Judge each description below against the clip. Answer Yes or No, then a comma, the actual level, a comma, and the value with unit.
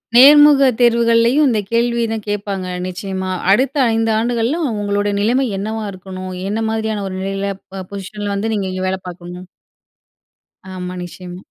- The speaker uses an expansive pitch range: No, average, 3.6 semitones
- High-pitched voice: Yes, high, 205 Hz